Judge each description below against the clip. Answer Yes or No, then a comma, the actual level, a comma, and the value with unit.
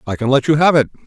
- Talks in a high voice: No, low, 135 Hz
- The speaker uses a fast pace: Yes, fast, 335 wpm